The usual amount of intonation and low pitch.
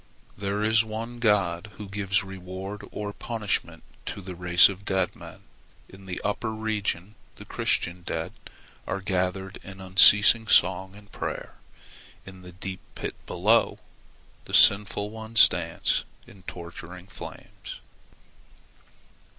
No: narrow, 2.1 semitones; low, 100 Hz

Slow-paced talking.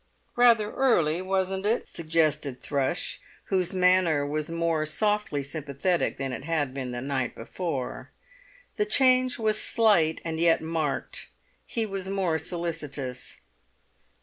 Yes: slow, 125 wpm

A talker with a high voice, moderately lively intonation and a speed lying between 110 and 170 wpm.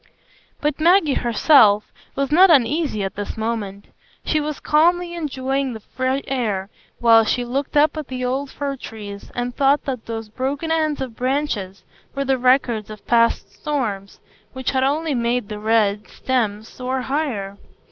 Yes: very high, 255 Hz; average, 4.4 semitones; average, 160 wpm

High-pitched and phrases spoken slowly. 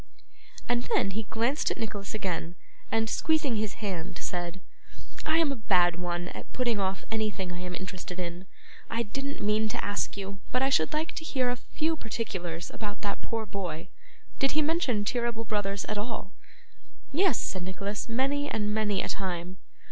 No: high, 210 Hz; average, 180 wpm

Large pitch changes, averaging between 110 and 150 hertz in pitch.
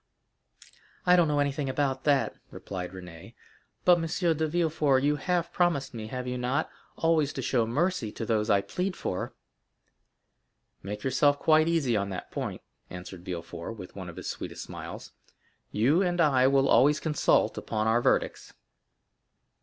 Yes: wide, 6.7 semitones; low, 135 Hz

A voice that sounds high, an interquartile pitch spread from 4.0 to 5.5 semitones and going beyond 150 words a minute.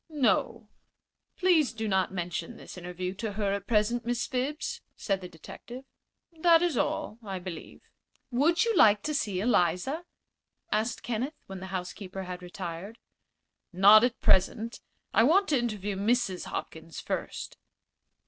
No: high, 215 Hz; average, 4.8 semitones; average, 145 wpm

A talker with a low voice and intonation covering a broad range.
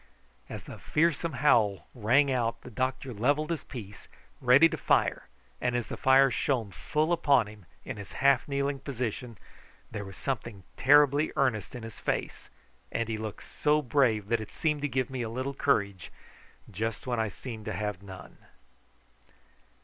No: low, 125 Hz; average, 4.3 semitones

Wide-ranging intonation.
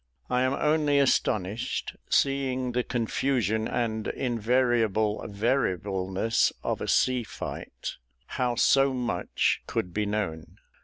No: average, 3.6 semitones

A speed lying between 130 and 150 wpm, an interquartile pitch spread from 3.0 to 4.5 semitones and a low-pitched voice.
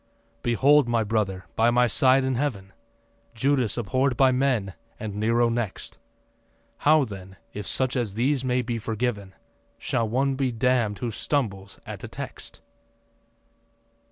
Yes: average, 140 wpm; average, 3.6 semitones; low, 120 Hz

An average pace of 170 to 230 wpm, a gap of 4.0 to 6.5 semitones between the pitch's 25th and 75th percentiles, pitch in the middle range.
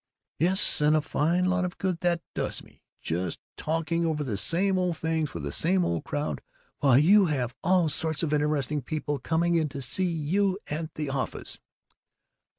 No: average, 180 wpm; average, 3.3 semitones; medium, 160 Hz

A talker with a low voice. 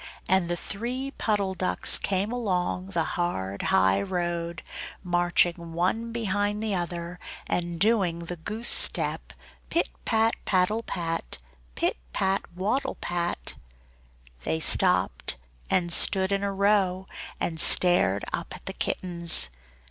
No: medium, 180 Hz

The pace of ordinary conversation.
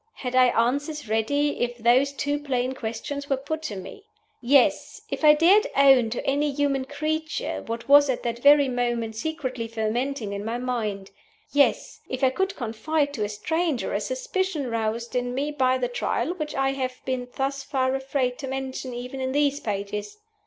Yes: average, 180 wpm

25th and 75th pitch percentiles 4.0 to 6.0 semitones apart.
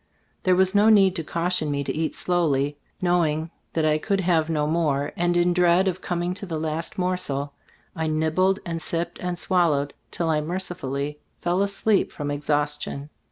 No: average, 3.2 semitones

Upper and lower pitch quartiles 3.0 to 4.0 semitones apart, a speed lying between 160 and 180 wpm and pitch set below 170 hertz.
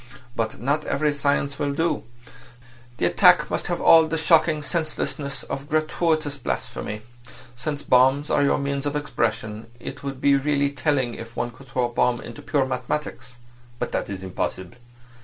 Yes: average, 3.5 semitones; average, 165 wpm; medium, 140 Hz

